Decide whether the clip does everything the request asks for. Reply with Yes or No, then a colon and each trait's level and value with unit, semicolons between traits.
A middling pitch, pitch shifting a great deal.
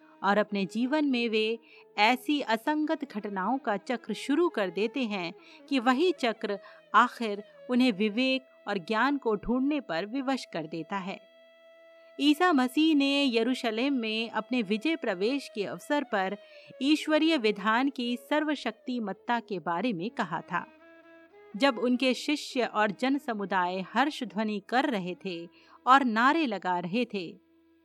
No: very high, 250 Hz; wide, 5.7 semitones